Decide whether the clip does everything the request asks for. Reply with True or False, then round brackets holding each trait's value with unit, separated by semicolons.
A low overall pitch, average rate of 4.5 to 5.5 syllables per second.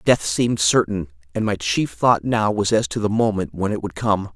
True (105 Hz; 5.1 syllables/s)